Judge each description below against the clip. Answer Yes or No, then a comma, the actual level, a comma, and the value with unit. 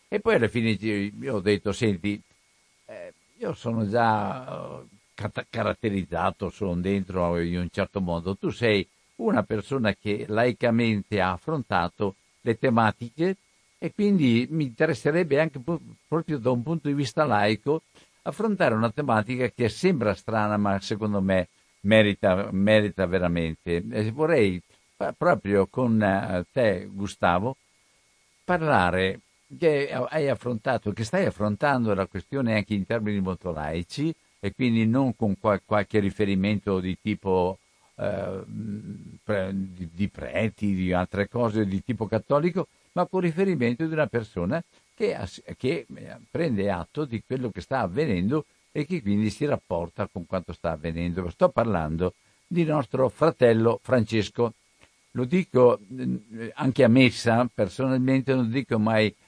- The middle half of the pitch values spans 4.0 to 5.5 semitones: Yes, average, 5.0 semitones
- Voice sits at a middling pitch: No, low, 110 Hz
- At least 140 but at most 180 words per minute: No, average, 130 wpm